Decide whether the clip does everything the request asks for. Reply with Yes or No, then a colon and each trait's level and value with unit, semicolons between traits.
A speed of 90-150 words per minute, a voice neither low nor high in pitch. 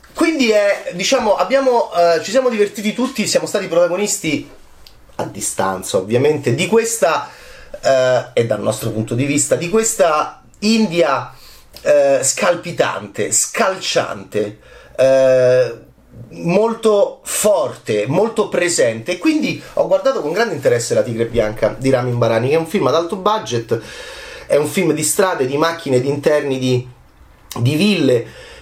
Yes: average, 140 wpm; medium, 170 Hz